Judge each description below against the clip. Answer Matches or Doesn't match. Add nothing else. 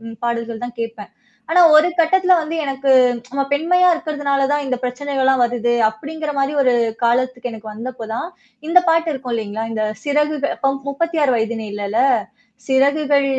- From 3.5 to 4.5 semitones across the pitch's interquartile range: Matches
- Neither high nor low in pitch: Doesn't match